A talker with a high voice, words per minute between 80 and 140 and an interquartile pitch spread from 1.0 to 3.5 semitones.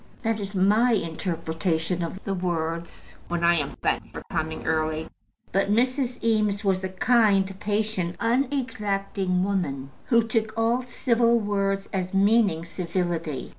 No: high, 195 Hz; slow, 135 wpm; average, 4.6 semitones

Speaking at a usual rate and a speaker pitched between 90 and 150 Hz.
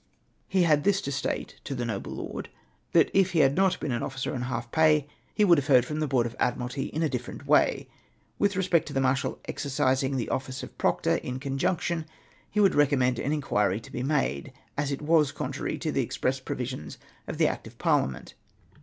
No: fast, 215 wpm; low, 135 Hz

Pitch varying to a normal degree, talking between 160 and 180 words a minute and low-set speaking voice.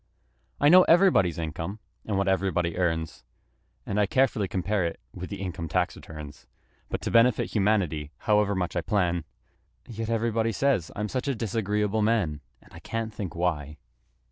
Yes: average, 4.5 semitones; average, 165 wpm; low, 100 Hz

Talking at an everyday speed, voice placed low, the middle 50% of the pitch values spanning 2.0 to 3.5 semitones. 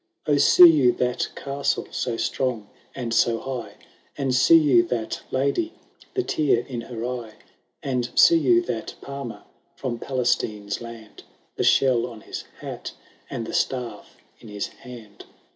Yes: average, 150 wpm; low, 125 Hz; average, 2.9 semitones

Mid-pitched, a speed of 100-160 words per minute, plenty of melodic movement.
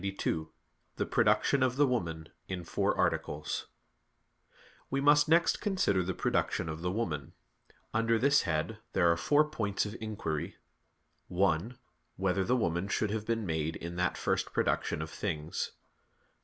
No: very low, 95 Hz; average, 155 wpm; wide, 5.9 semitones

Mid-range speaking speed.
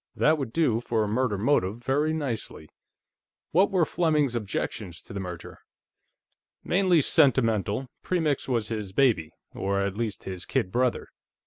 Yes: average, 145 wpm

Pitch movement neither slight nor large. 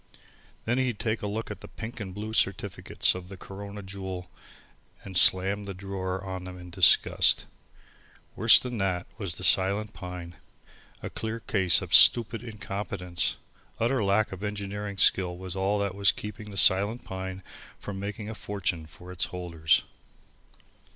No: narrow, 2.2 semitones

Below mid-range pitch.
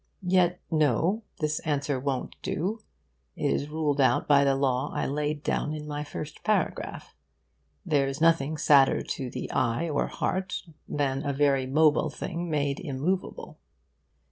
No: medium, 150 Hz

